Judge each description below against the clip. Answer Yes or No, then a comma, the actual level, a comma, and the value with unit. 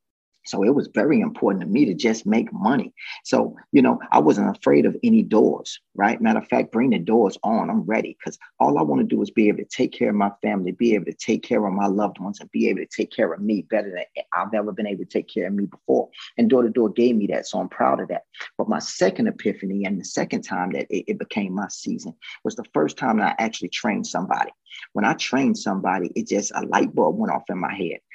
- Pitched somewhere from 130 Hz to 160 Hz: No, low, 105 Hz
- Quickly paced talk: Yes, fast, 260 wpm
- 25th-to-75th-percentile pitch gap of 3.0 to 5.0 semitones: Yes, average, 3.3 semitones